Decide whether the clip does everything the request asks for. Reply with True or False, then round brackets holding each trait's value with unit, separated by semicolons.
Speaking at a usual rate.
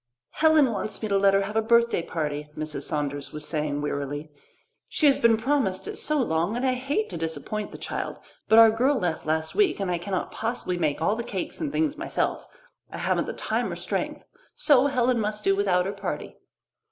False (210 wpm)